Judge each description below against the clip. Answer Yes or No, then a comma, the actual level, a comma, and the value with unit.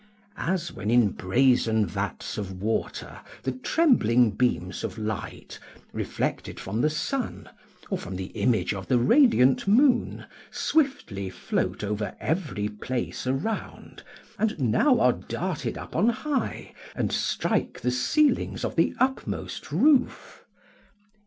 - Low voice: Yes, low, 125 Hz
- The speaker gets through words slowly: Yes, slow, 125 wpm